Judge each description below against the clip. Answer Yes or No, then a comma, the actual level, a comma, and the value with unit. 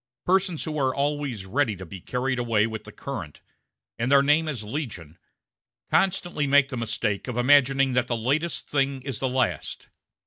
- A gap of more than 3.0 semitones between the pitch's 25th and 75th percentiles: Yes, average, 4.1 semitones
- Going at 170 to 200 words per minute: Yes, average, 175 wpm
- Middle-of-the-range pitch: No, low, 130 Hz